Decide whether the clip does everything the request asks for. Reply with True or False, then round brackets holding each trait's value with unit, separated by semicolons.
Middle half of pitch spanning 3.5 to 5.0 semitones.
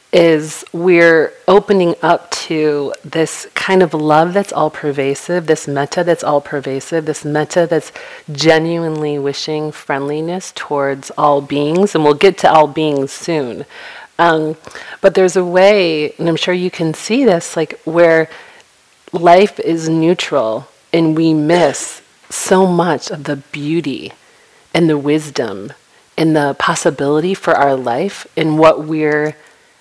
False (2.6 semitones)